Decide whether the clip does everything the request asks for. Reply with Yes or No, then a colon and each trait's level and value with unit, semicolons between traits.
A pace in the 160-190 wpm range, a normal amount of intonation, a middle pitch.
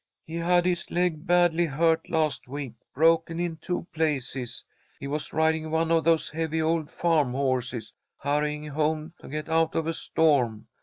No: average, 165 wpm; narrow, 2.2 semitones; medium, 160 Hz